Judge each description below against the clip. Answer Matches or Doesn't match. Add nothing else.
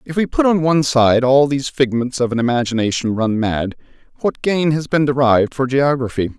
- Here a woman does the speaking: Doesn't match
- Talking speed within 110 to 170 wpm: Doesn't match